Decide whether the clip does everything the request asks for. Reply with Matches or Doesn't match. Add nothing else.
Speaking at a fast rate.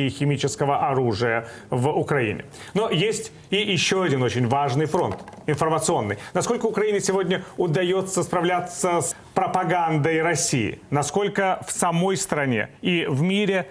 Doesn't match